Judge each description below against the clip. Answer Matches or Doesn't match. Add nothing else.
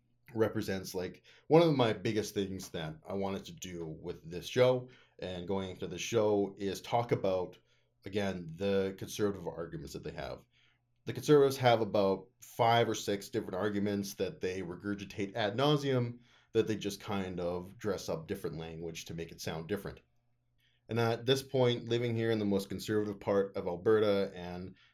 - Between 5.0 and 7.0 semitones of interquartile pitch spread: Doesn't match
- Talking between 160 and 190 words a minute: Matches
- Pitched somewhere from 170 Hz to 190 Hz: Doesn't match